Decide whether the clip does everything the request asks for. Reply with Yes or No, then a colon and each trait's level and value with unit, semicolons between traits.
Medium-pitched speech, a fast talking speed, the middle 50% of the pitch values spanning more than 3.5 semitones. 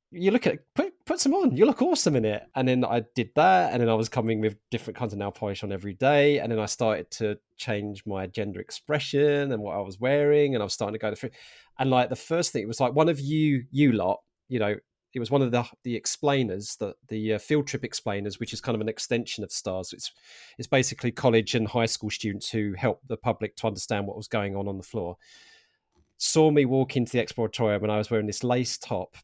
No: low, 115 Hz; fast, 250 wpm; average, 4.0 semitones